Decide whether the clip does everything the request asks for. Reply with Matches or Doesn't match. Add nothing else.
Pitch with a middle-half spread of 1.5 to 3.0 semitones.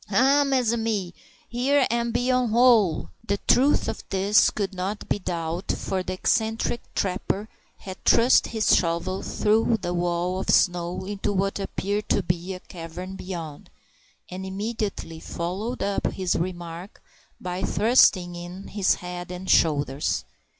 Doesn't match